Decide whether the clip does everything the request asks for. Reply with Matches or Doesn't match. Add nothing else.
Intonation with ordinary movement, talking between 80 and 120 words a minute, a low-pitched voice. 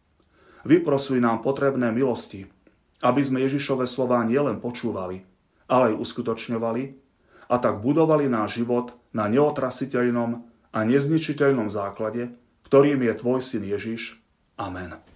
Matches